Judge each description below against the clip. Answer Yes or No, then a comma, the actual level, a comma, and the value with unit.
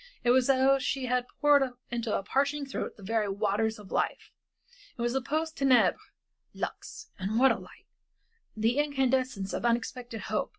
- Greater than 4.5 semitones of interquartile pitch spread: No, average, 3.5 semitones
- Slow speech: No, average, 175 wpm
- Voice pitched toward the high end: Yes, very high, 250 Hz